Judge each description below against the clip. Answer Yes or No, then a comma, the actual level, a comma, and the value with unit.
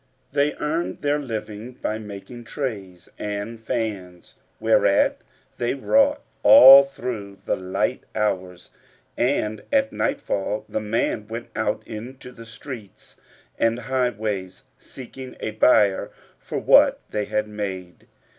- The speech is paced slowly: Yes, slow, 120 wpm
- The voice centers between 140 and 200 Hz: No, low, 110 Hz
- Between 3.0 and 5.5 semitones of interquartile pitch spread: Yes, average, 3.9 semitones